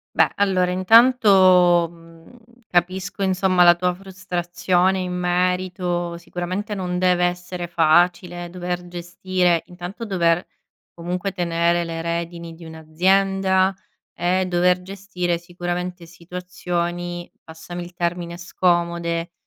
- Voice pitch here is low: No, medium, 180 Hz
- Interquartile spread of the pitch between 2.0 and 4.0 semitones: No, narrow, 1.1 semitones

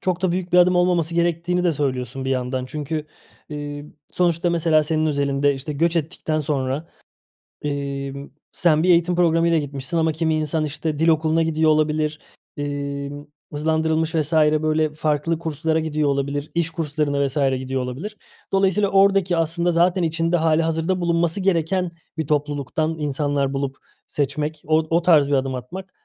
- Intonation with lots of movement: No, average, 2.7 semitones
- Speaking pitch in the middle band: Yes, medium, 155 Hz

